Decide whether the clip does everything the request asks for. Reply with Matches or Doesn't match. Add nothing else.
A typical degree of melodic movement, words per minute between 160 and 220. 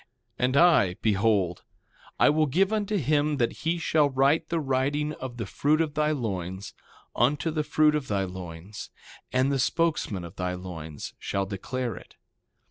Doesn't match